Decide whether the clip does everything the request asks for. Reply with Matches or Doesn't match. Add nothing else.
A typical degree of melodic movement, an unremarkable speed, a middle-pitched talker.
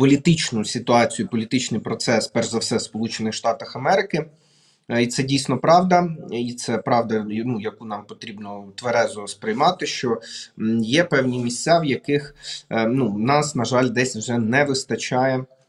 Doesn't match